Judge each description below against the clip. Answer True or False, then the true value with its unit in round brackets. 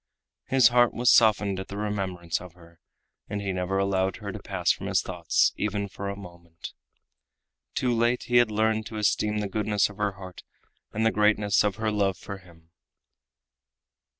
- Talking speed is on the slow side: False (180 wpm)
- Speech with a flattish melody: True (2.3 semitones)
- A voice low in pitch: True (100 Hz)